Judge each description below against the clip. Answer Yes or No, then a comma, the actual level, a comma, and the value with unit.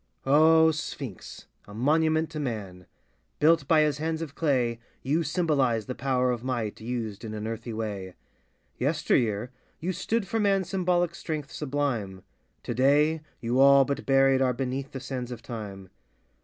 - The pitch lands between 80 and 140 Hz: Yes, low, 135 Hz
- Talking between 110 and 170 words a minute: Yes, average, 155 wpm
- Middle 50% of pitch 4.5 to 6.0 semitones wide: Yes, average, 5.1 semitones